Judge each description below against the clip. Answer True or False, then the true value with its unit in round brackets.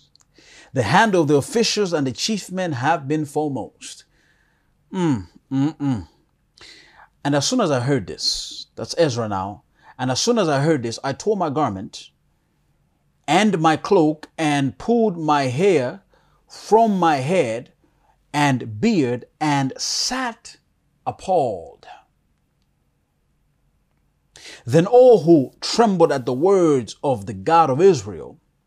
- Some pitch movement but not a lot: False (6.4 semitones)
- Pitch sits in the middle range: True (145 Hz)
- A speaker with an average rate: False (130 wpm)